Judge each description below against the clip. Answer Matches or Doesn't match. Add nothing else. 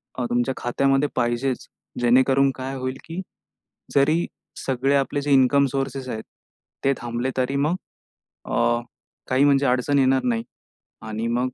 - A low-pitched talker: Matches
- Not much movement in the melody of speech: Matches